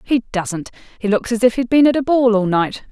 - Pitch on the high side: Yes, high, 230 Hz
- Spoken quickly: Yes, fast, 265 wpm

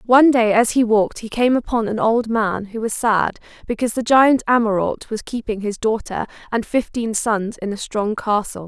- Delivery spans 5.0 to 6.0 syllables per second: Yes, 5.1 syllables/s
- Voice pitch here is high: Yes, high, 225 Hz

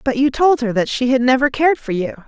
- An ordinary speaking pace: No, fast, 290 wpm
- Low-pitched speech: No, very high, 255 Hz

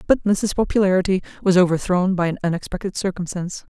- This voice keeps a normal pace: Yes, average, 145 wpm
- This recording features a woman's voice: Yes, female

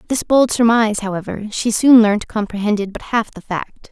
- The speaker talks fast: No, average, 185 wpm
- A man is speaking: No, female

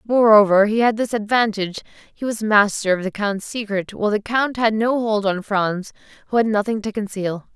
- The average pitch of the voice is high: Yes, high, 210 Hz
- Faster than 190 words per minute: Yes, average, 200 wpm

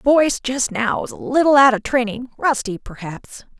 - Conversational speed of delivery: Yes, average, 185 wpm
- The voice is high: Yes, very high, 255 Hz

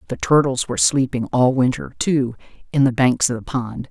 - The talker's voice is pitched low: Yes, low, 120 Hz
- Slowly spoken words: No, average, 200 wpm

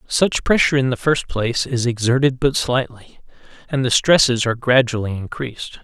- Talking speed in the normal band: Yes, average, 165 wpm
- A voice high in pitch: No, low, 125 Hz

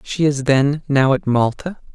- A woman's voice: No, male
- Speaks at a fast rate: No, average, 185 wpm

